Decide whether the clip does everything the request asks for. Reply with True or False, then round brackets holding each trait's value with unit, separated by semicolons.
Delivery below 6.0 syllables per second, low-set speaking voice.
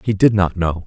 True (5.2 syllables/s; 95 Hz)